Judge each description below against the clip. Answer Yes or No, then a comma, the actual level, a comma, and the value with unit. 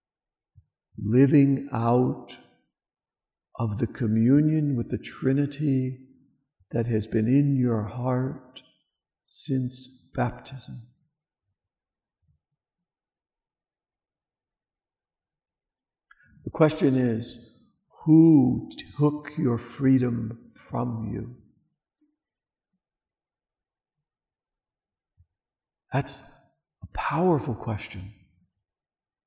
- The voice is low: Yes, low, 125 Hz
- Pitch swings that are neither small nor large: Yes, average, 4.0 semitones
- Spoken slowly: Yes, slow, 60 wpm